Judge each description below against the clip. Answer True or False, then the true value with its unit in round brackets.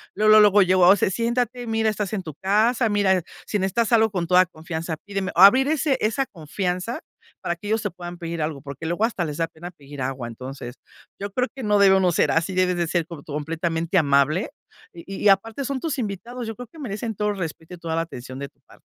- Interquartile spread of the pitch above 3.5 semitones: True (4.9 semitones)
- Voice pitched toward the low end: False (185 Hz)